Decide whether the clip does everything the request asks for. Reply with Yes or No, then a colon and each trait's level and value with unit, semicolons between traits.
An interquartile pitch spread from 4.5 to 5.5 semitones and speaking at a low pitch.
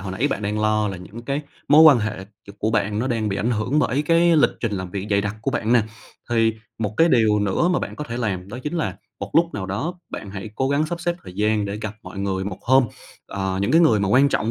Yes: average, 5.0 semitones; low, 110 Hz